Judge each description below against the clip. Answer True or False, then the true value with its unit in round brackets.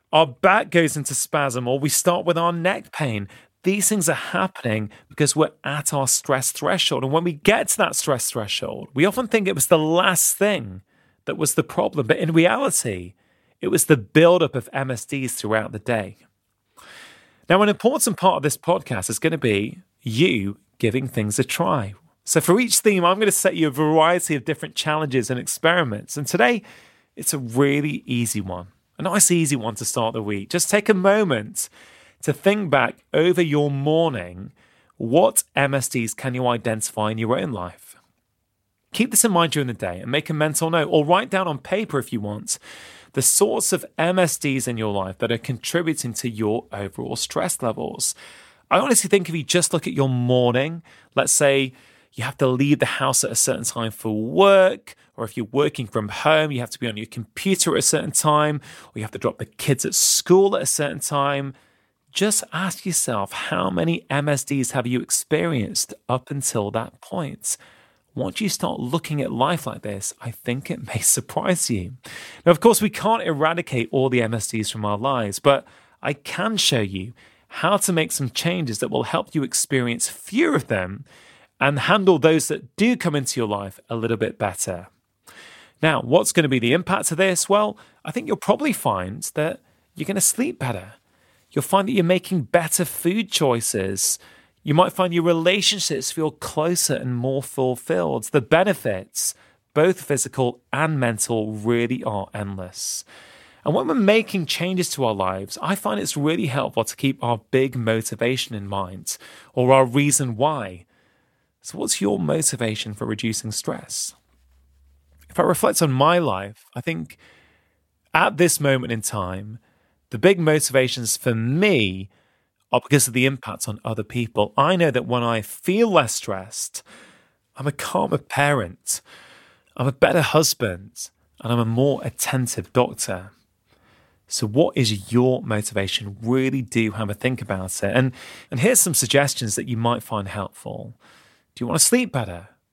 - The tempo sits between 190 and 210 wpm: False (180 wpm)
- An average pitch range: False (6.8 semitones)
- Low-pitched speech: True (130 Hz)